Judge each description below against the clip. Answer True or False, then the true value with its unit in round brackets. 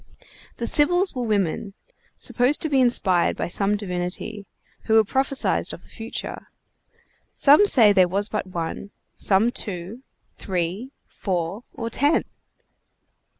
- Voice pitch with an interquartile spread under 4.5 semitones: False (5.0 semitones)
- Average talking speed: False (125 wpm)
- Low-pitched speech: False (210 Hz)